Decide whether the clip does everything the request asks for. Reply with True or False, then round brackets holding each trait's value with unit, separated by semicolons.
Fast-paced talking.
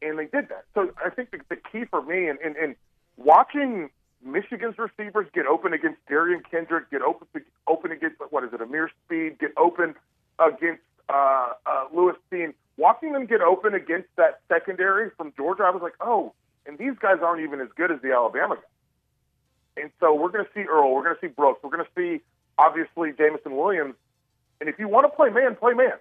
True (210 wpm)